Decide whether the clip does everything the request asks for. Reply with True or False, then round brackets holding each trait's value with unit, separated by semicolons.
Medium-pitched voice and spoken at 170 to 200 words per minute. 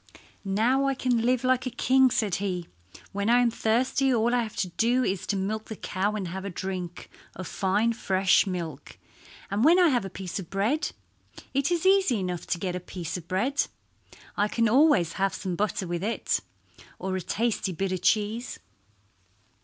False (210 Hz; 185 wpm)